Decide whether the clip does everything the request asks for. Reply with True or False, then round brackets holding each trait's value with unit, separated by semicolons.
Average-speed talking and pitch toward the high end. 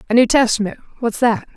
True (190 wpm; 235 Hz)